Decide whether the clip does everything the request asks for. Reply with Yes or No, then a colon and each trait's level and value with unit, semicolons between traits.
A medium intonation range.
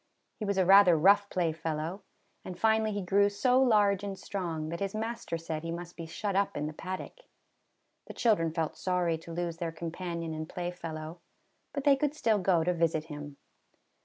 Yes: average, 3.6 semitones